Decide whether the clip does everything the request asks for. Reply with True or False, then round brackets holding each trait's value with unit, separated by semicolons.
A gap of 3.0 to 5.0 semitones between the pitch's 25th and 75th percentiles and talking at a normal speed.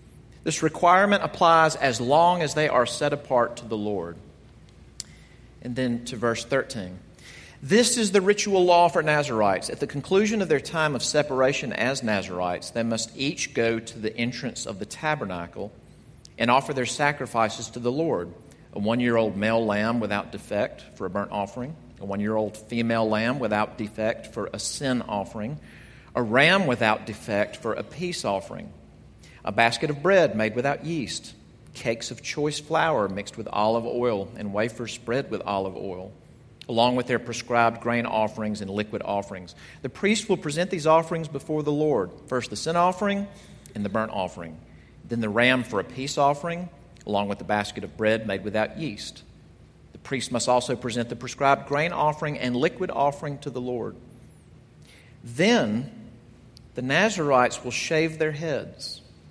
False (5.5 semitones; 170 wpm)